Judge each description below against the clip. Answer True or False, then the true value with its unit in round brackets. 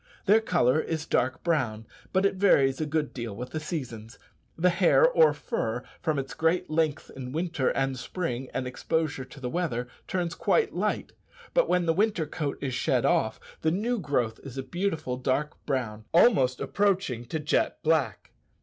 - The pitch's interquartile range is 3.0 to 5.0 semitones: False (5.6 semitones)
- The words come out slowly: False (175 wpm)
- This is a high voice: False (150 Hz)